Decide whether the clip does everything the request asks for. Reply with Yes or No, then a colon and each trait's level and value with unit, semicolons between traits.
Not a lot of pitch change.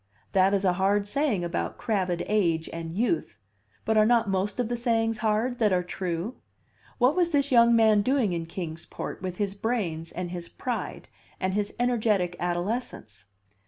No: average, 4.7 semitones